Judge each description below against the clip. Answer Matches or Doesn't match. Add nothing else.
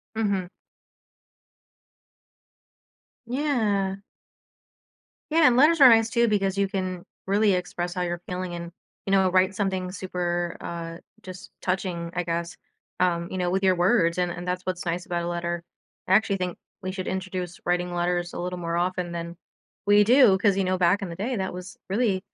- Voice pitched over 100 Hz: Matches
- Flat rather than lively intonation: Matches